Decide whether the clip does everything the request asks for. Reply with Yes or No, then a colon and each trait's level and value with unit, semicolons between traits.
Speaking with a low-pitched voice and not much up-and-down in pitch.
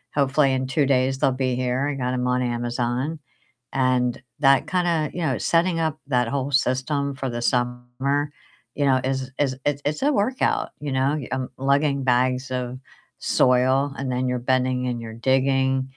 Yes: low, 130 Hz; narrow, 1.9 semitones